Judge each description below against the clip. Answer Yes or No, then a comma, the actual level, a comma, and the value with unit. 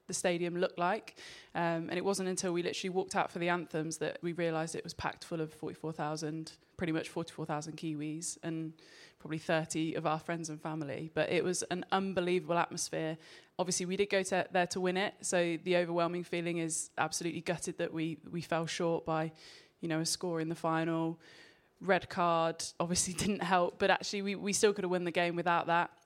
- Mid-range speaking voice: Yes, medium, 170 Hz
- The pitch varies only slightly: Yes, narrow, 2.1 semitones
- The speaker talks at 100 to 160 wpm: No, fast, 205 wpm